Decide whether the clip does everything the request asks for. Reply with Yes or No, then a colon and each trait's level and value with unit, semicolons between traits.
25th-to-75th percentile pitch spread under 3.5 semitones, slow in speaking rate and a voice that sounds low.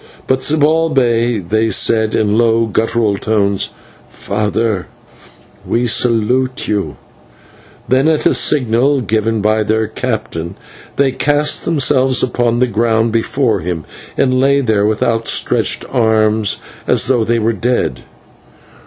Yes: average, 3.0 semitones; slow, 125 wpm; low, 115 Hz